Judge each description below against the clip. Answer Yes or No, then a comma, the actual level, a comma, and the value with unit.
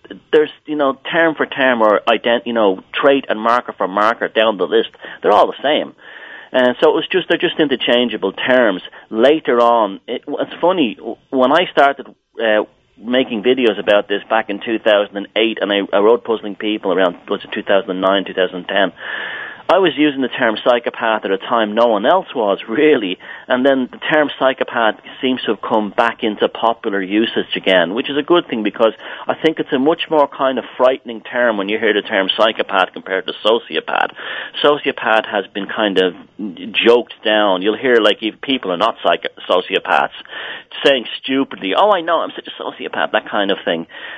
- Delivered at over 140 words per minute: Yes, average, 200 wpm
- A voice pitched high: No, low, 120 Hz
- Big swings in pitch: No, average, 4.6 semitones